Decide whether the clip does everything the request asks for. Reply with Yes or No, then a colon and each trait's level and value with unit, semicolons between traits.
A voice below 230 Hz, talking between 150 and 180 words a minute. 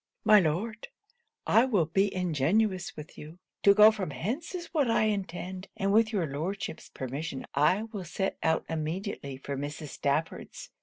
Yes: medium, 185 Hz; average, 160 wpm